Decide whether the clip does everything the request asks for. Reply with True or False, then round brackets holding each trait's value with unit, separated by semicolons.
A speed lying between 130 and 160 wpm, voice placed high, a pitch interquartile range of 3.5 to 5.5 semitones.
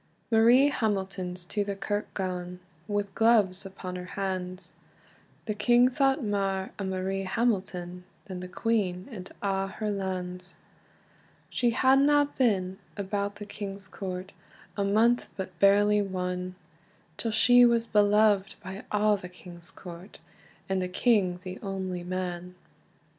False (135 wpm; 195 Hz; 2.6 semitones)